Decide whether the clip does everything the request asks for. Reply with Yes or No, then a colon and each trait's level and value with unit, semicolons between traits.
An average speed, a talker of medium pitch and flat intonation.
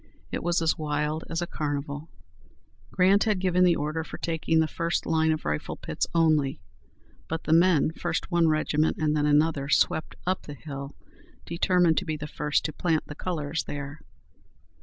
Yes: average, 180 wpm; medium, 160 Hz; narrow, 2.2 semitones